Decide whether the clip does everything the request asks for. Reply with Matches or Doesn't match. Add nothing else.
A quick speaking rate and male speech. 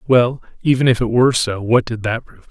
Matches